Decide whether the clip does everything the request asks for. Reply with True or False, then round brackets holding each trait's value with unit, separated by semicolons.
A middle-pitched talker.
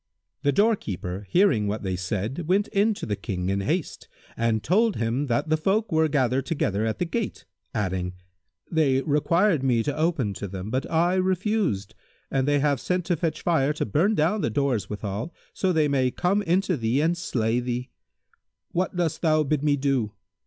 True (145 Hz)